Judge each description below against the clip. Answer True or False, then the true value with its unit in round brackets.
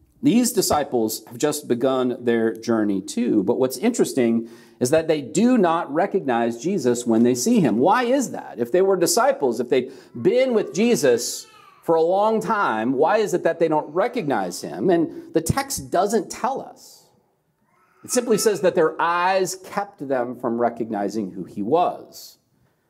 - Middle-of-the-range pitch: True (165 Hz)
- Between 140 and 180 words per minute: True (170 wpm)